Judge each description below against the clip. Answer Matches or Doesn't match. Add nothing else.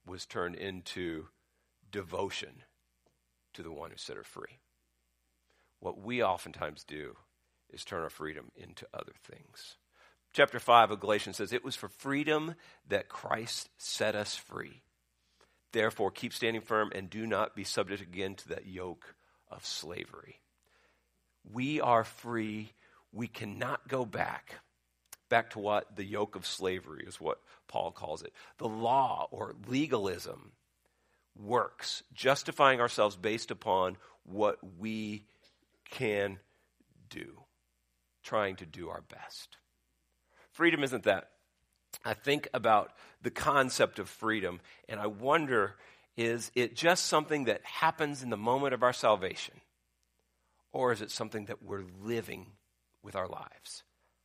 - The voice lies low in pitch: Matches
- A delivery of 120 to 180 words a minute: Matches